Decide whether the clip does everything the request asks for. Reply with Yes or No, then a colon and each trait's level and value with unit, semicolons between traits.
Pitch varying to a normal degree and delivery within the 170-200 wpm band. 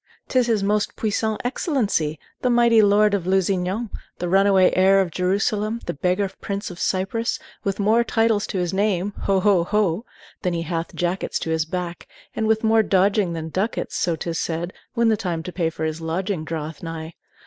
Yes: average, 3.7 semitones; average, 195 wpm